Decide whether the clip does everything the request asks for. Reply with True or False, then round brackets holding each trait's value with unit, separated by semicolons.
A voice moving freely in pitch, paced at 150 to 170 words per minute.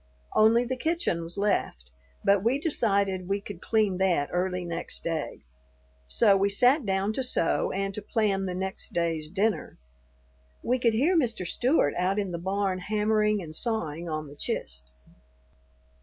False (4.0 semitones; 160 wpm)